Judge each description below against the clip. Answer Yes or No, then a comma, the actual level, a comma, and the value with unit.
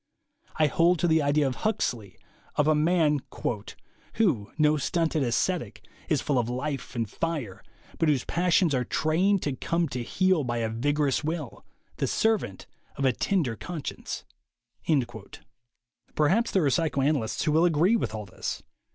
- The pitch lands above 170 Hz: No, medium, 150 Hz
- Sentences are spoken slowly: No, average, 155 wpm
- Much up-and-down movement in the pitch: No, average, 4.8 semitones